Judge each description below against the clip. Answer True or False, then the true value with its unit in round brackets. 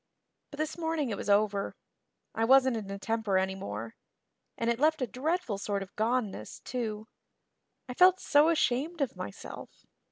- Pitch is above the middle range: True (235 Hz)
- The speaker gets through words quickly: False (160 wpm)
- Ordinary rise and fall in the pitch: False (6.5 semitones)